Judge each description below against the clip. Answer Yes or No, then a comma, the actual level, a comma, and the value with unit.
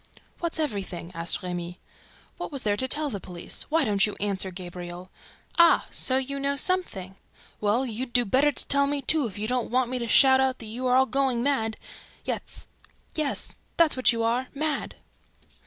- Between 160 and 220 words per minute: Yes, average, 190 wpm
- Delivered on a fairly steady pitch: No, wide, 5.5 semitones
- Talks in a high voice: Yes, very high, 250 Hz